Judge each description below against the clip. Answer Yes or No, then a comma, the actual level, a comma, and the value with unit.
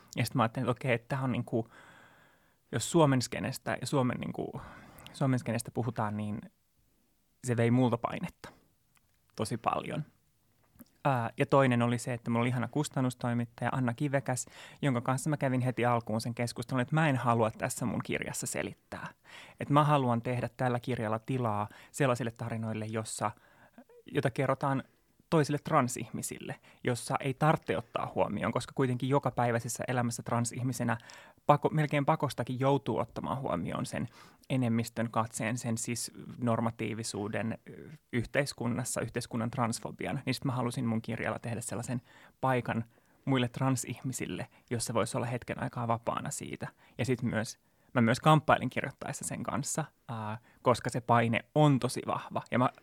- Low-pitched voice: Yes, low, 120 Hz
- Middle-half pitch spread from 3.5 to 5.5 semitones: No, narrow, 2.4 semitones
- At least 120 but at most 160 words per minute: Yes, average, 140 wpm